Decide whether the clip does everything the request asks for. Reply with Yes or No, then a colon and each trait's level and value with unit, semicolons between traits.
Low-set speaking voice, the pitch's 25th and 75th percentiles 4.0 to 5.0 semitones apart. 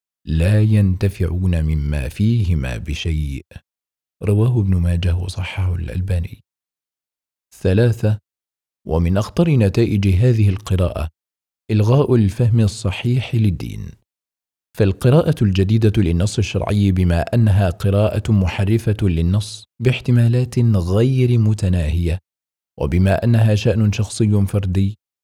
Yes: low, 100 Hz; average, 4.4 semitones